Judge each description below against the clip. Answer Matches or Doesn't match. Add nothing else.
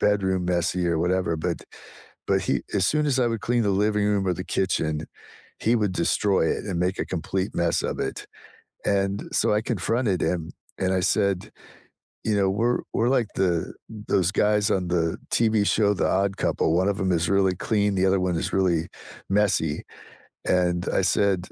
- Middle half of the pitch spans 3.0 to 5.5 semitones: Doesn't match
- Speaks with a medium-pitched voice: Doesn't match